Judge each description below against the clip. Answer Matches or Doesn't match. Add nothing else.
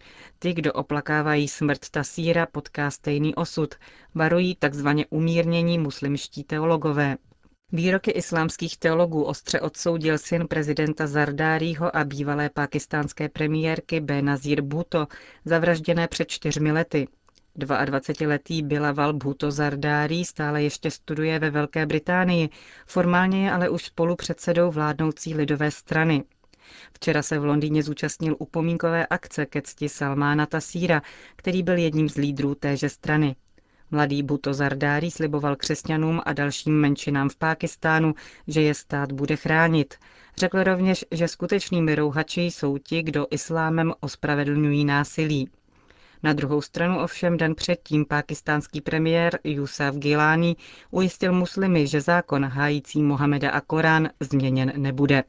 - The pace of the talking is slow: Doesn't match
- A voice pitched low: Doesn't match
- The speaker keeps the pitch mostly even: Matches